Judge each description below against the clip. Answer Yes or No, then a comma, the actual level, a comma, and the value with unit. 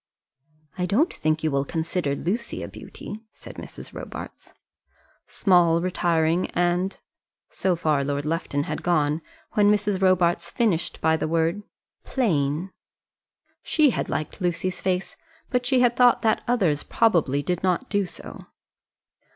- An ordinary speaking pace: Yes, average, 145 wpm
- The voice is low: No, medium, 175 Hz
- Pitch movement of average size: Yes, average, 4.3 semitones